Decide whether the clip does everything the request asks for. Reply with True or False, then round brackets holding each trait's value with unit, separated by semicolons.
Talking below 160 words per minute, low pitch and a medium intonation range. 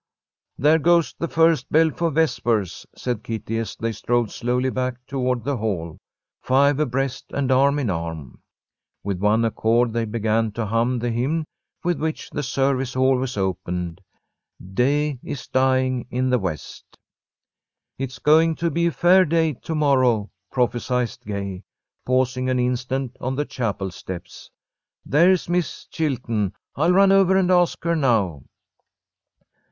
True (145 wpm; 130 Hz; 4.7 semitones)